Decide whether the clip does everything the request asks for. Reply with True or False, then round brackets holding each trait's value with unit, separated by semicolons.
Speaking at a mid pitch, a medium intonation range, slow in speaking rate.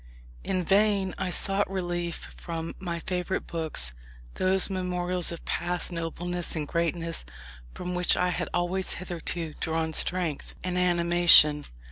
False (175 Hz; 1.5 semitones; 130 wpm)